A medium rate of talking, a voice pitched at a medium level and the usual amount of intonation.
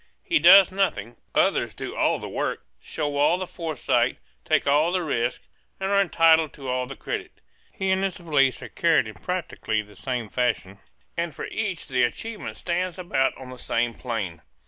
No: average, 185 wpm; medium, 150 Hz; wide, 6.5 semitones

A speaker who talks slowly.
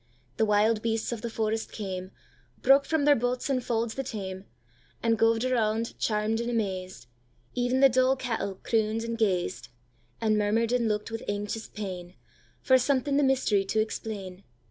No: average, 145 wpm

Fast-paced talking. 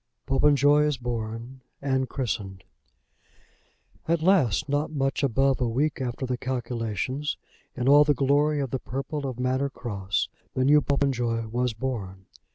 No: average, 145 wpm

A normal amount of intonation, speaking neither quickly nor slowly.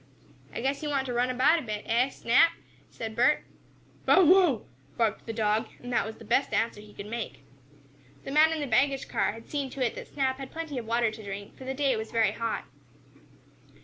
No: average, 3.8 semitones; fast, 220 wpm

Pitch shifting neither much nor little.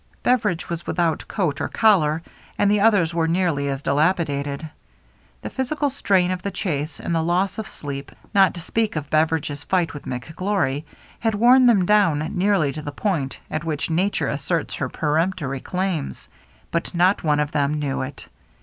Yes: average, 4.8 semitones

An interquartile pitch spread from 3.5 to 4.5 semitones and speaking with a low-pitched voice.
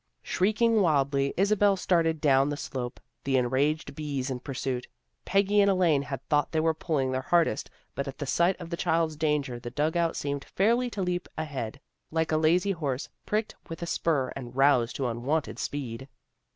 No: average, 4.1 semitones; medium, 150 Hz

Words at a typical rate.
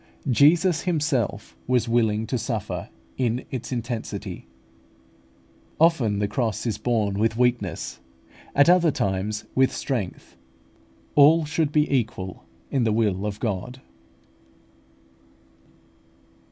No: slow, 115 wpm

